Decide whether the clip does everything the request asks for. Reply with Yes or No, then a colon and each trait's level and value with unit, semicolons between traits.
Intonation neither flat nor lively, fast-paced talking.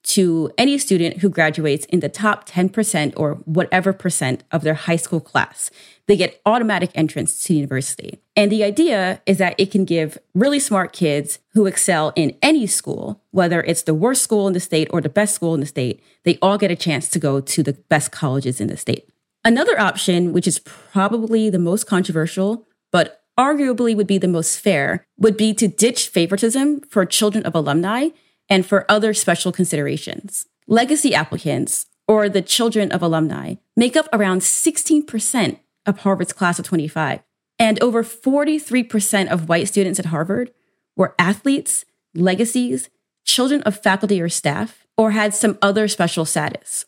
No: average, 4.6 semitones; average, 175 wpm